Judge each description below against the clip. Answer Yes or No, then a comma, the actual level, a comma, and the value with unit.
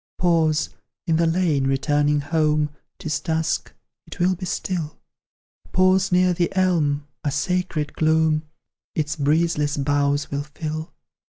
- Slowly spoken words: Yes, slow, 125 wpm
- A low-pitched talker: No, medium, 155 Hz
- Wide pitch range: No, average, 2.8 semitones